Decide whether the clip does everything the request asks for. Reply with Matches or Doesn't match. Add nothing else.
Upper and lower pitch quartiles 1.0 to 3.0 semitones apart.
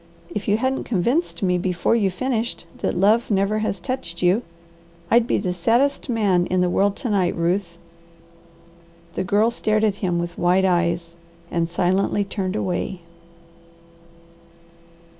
Doesn't match